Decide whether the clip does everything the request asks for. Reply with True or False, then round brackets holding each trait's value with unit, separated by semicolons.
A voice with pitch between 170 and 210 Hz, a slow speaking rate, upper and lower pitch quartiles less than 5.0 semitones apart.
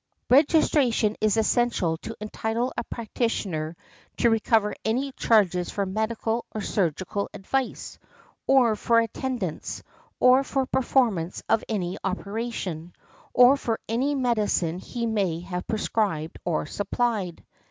False (220 Hz; 120 wpm; 4.3 semitones)